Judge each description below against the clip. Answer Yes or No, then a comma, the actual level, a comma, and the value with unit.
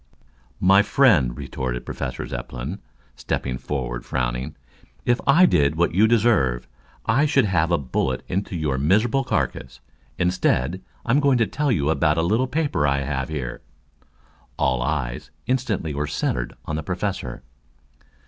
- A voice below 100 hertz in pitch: Yes, very low, 80 Hz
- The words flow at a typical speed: Yes, average, 145 wpm